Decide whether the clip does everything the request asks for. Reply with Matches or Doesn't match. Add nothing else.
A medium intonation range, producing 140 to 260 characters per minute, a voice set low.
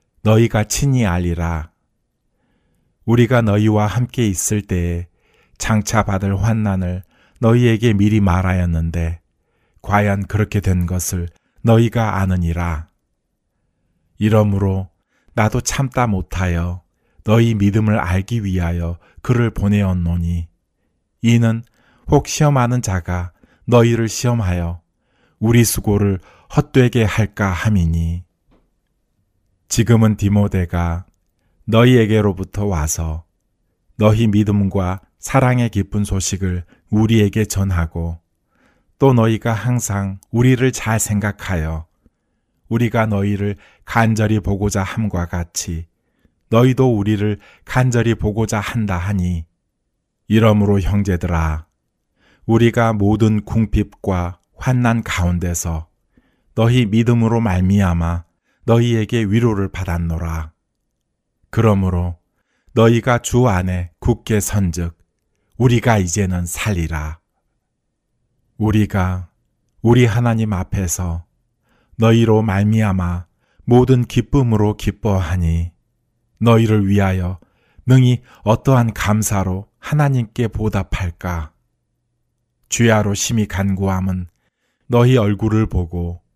Matches